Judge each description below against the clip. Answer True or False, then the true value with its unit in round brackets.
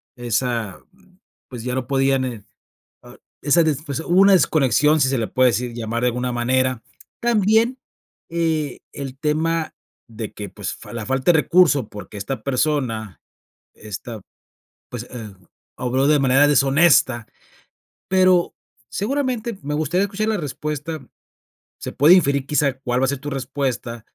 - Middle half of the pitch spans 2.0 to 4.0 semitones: False (4.6 semitones)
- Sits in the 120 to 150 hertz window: True (135 Hz)